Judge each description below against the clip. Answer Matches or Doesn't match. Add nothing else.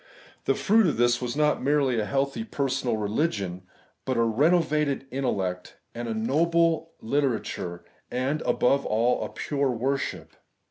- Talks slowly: Doesn't match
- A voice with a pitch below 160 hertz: Matches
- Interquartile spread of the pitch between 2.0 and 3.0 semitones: Doesn't match